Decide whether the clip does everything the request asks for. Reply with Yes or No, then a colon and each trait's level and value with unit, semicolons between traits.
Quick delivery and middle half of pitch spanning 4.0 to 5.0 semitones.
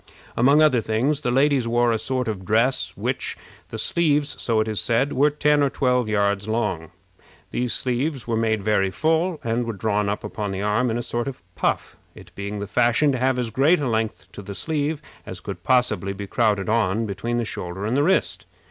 Yes: fast, 220 wpm; average, 4.3 semitones